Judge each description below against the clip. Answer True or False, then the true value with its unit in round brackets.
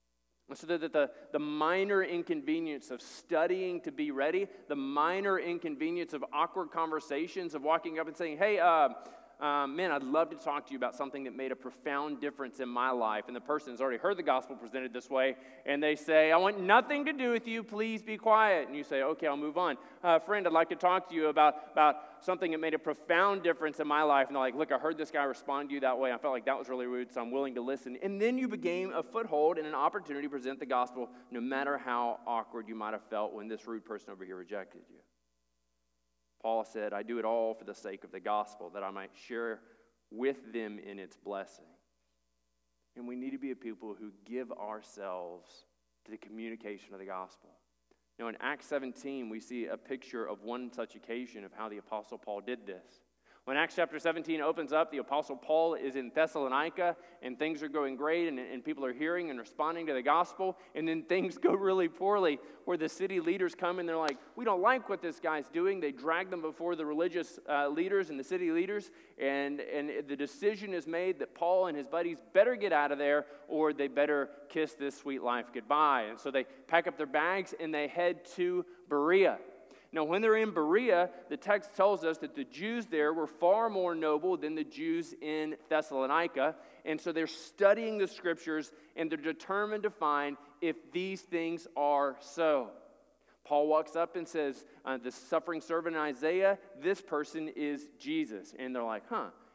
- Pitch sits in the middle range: True (150 Hz)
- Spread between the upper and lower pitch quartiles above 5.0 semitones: True (5.4 semitones)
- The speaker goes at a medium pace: False (215 wpm)